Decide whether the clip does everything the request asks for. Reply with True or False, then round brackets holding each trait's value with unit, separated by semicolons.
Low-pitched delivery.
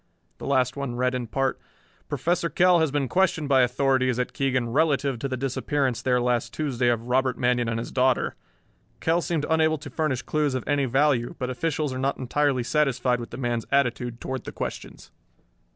True (130 Hz)